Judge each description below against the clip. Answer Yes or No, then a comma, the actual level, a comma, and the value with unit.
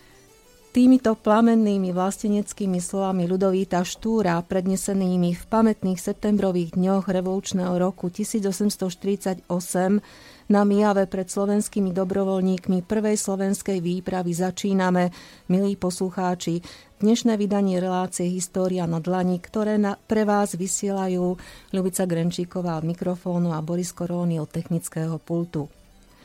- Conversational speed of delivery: No, slow, 105 wpm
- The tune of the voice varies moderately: No, narrow, 2.1 semitones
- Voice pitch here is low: No, high, 190 Hz